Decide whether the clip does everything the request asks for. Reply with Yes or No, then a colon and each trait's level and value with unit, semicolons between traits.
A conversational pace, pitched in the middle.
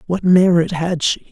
Yes: average, 185 wpm; medium, 175 Hz